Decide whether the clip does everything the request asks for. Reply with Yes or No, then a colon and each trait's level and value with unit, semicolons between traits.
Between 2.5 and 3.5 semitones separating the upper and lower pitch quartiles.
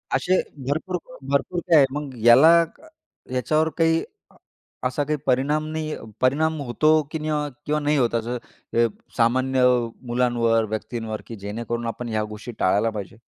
No: average, 4.7 semitones